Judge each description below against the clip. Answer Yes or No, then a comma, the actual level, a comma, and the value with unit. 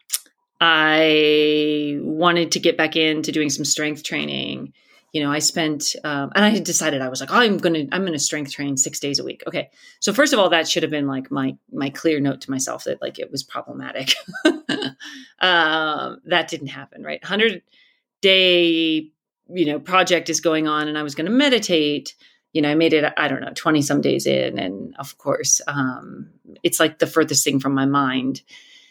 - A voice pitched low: No, medium, 155 Hz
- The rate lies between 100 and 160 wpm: No, average, 195 wpm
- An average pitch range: Yes, average, 3.5 semitones